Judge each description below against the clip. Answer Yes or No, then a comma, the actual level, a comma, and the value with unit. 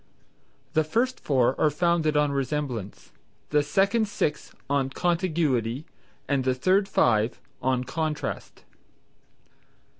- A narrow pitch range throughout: No, average, 4.7 semitones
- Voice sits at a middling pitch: Yes, medium, 150 Hz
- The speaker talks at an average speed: No, slow, 110 wpm